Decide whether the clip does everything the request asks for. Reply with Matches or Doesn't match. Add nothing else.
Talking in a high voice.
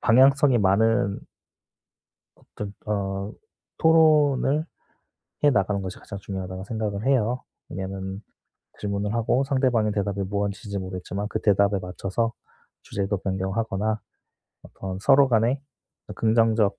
Doesn't match